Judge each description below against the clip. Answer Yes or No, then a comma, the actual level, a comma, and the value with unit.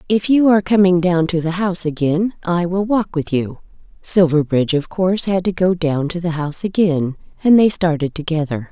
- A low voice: No, medium, 175 Hz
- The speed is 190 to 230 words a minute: Yes, average, 200 wpm